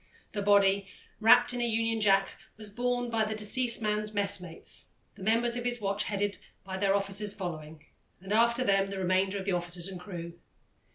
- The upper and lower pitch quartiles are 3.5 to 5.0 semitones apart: No, narrow, 2.6 semitones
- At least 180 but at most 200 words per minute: Yes, average, 185 wpm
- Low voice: No, high, 200 Hz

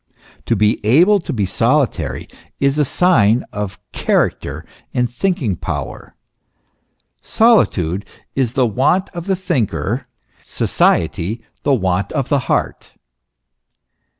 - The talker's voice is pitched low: Yes, low, 125 Hz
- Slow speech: Yes, slow, 115 wpm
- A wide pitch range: Yes, wide, 6.6 semitones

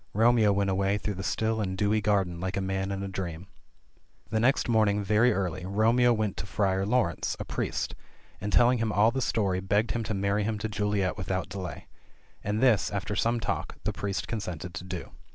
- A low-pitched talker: Yes, low, 100 Hz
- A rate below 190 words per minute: No, fast, 205 wpm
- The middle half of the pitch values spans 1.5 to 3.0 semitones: Yes, narrow, 2.4 semitones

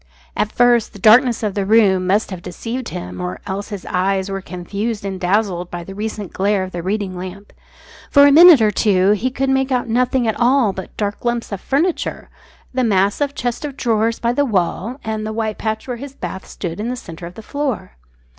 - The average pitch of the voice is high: Yes, high, 215 Hz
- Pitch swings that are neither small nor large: Yes, average, 4.3 semitones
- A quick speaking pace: Yes, fast, 220 wpm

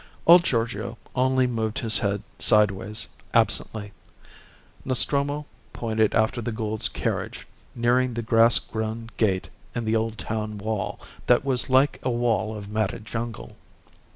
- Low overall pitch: Yes, low, 115 Hz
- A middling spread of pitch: No, narrow, 2.0 semitones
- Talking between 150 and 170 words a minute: No, slow, 135 wpm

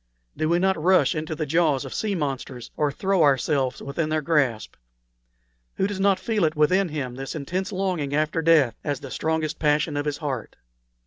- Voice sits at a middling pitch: Yes, medium, 155 Hz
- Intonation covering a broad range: No, average, 3.7 semitones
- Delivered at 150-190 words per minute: Yes, average, 185 wpm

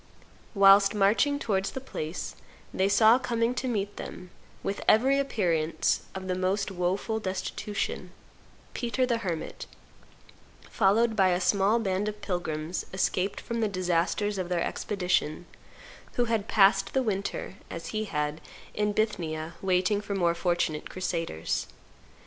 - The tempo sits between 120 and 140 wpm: Yes, slow, 135 wpm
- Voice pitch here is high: Yes, high, 195 Hz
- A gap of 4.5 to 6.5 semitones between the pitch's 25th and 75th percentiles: No, average, 3.3 semitones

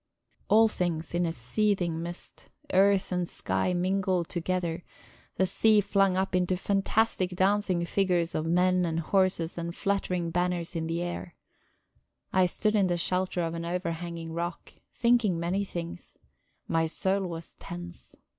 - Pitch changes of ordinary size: No, narrow, 2.1 semitones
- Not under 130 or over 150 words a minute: Yes, average, 145 wpm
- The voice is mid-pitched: Yes, medium, 180 Hz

